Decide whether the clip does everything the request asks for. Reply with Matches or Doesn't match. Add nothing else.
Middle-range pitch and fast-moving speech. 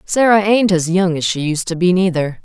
Matches